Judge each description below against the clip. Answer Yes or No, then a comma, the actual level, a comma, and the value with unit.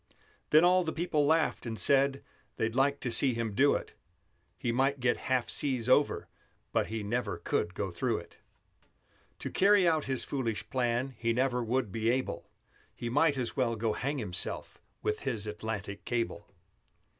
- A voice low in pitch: Yes, low, 125 Hz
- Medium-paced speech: Yes, average, 170 wpm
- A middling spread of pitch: Yes, average, 3.7 semitones